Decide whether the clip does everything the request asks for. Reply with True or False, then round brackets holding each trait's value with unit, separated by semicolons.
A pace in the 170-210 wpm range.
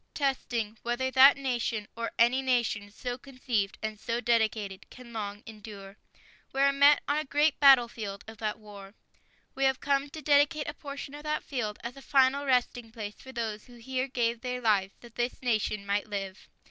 True (185 wpm)